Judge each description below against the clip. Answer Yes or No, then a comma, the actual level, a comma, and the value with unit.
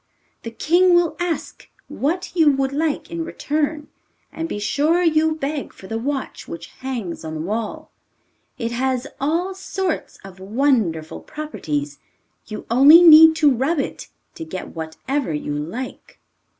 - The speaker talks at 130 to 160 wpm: Yes, average, 150 wpm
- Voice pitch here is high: Yes, very high, 275 Hz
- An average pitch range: No, wide, 7.3 semitones